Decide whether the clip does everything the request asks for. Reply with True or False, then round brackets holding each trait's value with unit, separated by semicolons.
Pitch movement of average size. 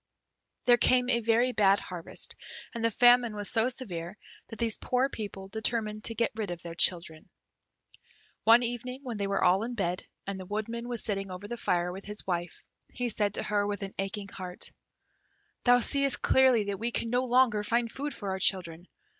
True (3.7 semitones)